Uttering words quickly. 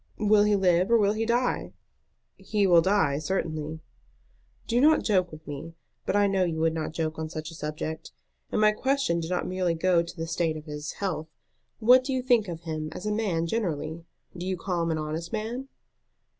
Yes: fast, 210 wpm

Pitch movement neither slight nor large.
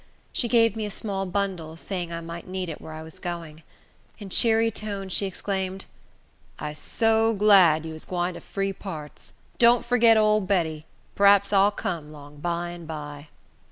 Yes: average, 4.2 semitones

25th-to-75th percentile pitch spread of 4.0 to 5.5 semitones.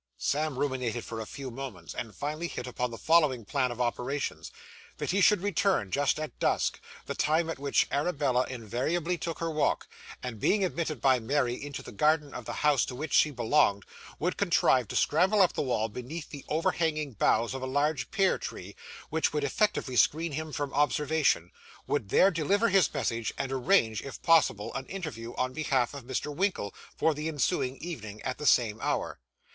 Yes: average, 4.4 semitones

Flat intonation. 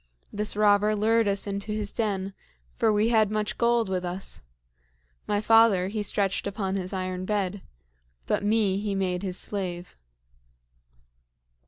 Yes: narrow, 2.1 semitones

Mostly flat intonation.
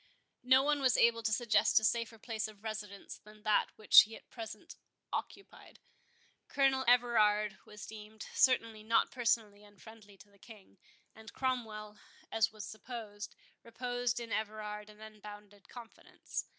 Yes: narrow, 2.0 semitones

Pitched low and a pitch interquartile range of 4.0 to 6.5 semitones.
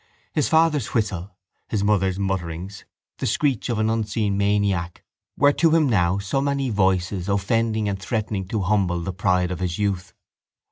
No: low, 100 Hz; average, 3.2 semitones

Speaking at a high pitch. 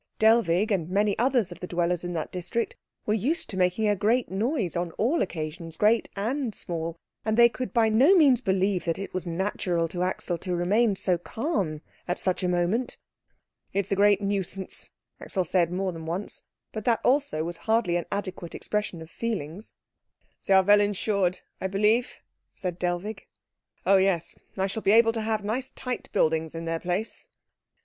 Yes: high, 195 Hz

